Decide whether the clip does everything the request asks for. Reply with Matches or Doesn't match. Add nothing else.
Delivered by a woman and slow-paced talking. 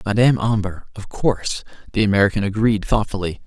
Doesn't match